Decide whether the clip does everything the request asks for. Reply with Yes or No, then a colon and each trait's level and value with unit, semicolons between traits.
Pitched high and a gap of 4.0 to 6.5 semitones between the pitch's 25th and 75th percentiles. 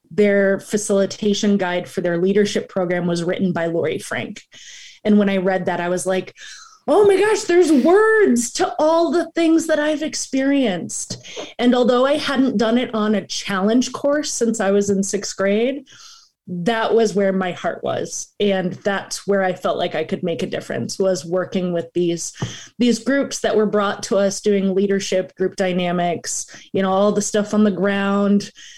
Yes: high, 205 Hz; average, 4.7 semitones